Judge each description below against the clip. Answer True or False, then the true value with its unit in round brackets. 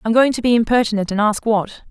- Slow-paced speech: False (250 wpm)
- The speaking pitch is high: True (220 Hz)